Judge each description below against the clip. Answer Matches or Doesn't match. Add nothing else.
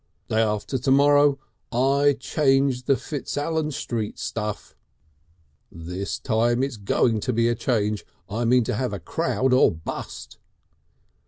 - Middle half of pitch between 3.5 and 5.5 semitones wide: Matches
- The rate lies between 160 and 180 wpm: Doesn't match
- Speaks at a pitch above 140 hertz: Doesn't match